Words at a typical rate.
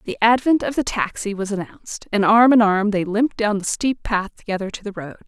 No: fast, 240 wpm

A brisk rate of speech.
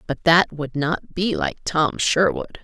No: average, 185 wpm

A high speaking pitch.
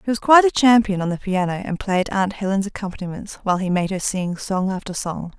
Yes: high, 195 Hz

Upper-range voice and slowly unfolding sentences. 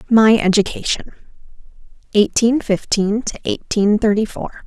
Yes: high, 215 Hz; slow, 105 wpm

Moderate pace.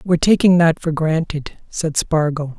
Yes: average, 160 wpm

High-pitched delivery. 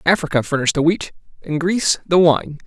No: medium, 160 Hz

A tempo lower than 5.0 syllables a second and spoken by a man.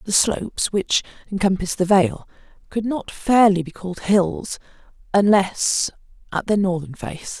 No: 4.5 syllables/s; female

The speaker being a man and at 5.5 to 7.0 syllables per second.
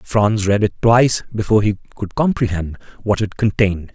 Yes: male; 5.6 syllables/s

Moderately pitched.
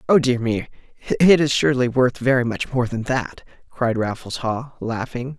No: low, 125 Hz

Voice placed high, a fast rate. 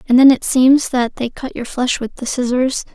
Yes: very high, 255 Hz; fast, 245 wpm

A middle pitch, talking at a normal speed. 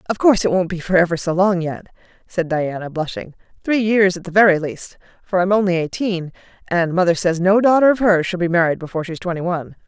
No: medium, 180 Hz; fast, 225 wpm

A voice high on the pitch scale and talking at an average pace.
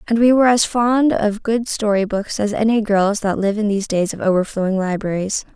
No: high, 210 Hz; fast, 215 wpm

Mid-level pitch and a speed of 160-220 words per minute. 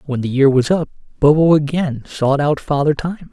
Yes: medium, 145 Hz; average, 200 wpm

